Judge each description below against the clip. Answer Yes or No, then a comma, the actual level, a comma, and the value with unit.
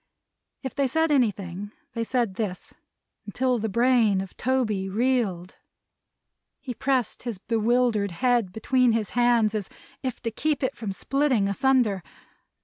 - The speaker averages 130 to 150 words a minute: Yes, average, 140 wpm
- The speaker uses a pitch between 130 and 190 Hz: No, high, 230 Hz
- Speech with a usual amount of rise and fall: Yes, average, 3.9 semitones